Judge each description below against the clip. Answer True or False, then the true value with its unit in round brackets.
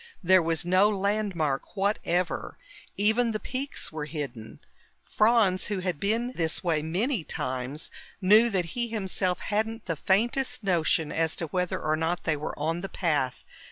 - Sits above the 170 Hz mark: True (185 Hz)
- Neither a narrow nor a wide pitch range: True (4.8 semitones)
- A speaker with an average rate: True (160 wpm)